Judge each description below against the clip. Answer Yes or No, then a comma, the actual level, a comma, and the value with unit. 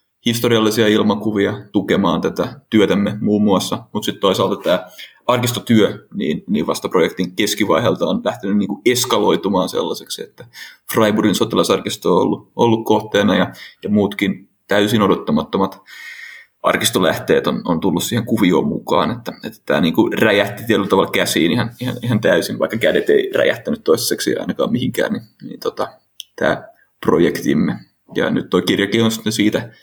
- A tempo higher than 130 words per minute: Yes, average, 145 wpm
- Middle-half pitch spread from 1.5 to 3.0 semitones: Yes, average, 2.7 semitones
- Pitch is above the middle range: No, low, 110 Hz